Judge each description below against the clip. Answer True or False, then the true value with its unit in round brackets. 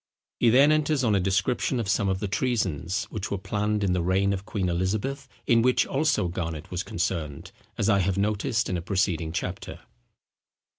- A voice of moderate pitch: False (100 Hz)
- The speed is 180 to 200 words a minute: True (190 wpm)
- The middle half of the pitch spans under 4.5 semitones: True (3.7 semitones)